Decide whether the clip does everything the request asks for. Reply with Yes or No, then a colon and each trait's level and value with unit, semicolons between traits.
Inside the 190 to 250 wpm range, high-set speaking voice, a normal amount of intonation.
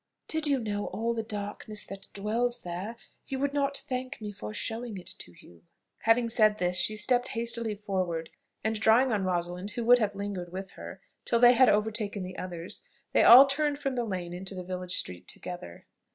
Yes: average, 195 wpm; high, 210 Hz; average, 4.7 semitones